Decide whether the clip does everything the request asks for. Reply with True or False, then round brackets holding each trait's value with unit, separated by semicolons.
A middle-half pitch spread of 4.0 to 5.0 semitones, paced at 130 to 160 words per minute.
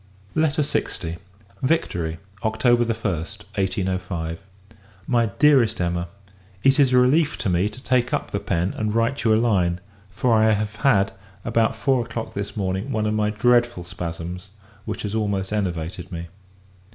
True (4.7 semitones; 155 wpm)